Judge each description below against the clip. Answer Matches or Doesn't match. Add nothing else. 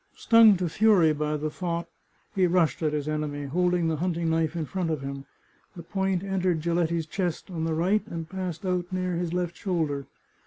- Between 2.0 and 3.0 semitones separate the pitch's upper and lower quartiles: Matches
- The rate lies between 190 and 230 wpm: Matches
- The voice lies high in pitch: Doesn't match